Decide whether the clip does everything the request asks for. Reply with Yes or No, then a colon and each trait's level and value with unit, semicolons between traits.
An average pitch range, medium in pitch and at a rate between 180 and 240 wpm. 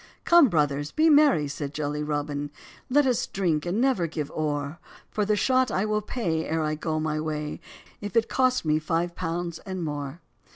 No: wide, 5.9 semitones; medium, 165 Hz; average, 190 wpm